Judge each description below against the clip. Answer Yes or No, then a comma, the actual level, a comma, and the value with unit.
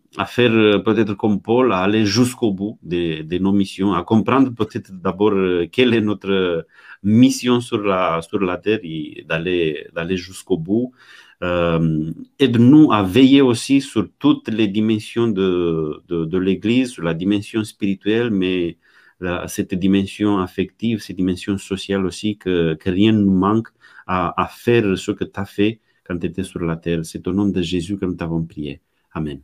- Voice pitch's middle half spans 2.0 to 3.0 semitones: No, average, 3.6 semitones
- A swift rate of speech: No, average, 180 wpm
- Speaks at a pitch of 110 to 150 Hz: No, low, 100 Hz